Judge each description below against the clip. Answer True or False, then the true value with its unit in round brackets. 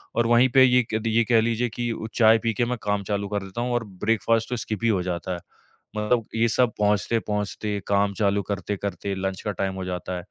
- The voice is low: True (105 Hz)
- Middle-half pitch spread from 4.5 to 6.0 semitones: False (2.8 semitones)